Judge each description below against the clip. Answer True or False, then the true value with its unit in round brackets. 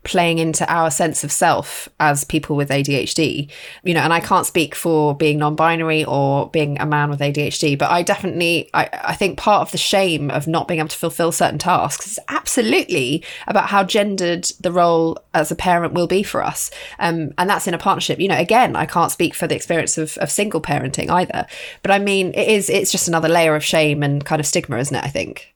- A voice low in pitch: False (165 Hz)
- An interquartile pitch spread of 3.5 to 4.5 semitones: False (2.9 semitones)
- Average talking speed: False (225 wpm)